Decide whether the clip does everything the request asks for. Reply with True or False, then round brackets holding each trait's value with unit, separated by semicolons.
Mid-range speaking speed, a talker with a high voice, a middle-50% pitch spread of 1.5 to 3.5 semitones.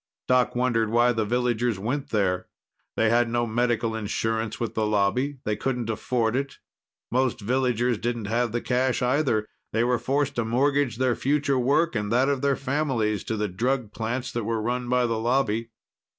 False (180 wpm; 120 Hz; 2.5 semitones)